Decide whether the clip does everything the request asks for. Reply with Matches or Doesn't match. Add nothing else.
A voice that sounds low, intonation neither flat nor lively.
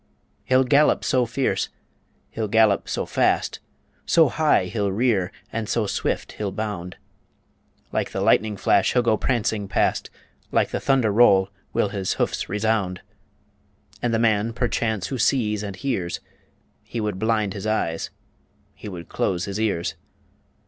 Matches